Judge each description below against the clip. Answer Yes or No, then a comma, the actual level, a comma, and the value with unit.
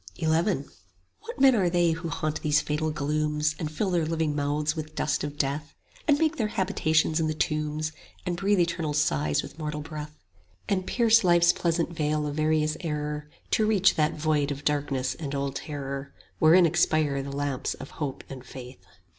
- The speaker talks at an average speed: Yes, average, 185 wpm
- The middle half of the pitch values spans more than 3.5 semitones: No, narrow, 2.6 semitones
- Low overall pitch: No, medium, 155 Hz